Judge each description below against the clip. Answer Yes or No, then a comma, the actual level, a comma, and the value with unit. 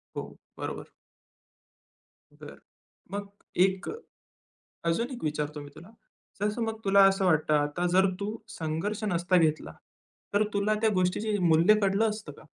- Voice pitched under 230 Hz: Yes, high, 190 Hz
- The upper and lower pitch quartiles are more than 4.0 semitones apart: Yes, average, 4.6 semitones